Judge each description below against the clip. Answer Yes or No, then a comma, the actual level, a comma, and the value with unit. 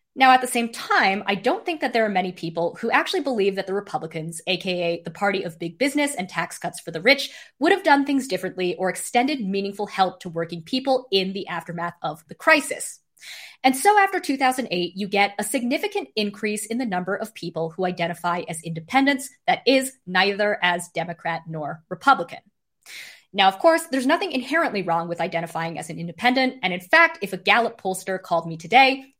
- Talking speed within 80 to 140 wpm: No, average, 195 wpm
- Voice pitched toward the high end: Yes, high, 200 Hz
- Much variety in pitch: Yes, wide, 7.2 semitones